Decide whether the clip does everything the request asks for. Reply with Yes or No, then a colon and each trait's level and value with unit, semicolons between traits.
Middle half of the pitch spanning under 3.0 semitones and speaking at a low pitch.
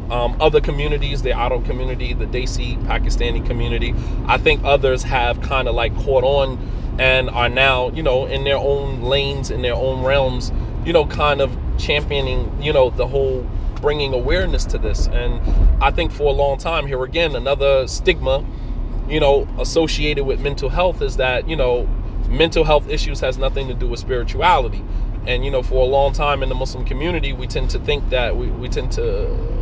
Yes: narrow, 2.6 semitones; low, 130 Hz